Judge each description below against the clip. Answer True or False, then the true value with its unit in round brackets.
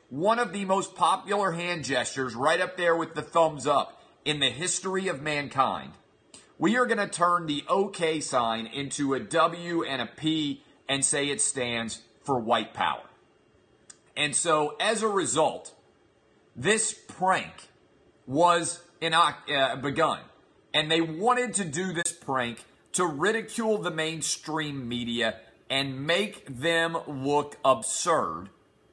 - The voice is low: False (160 Hz)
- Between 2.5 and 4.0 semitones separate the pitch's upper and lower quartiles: False (4.7 semitones)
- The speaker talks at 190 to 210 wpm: False (140 wpm)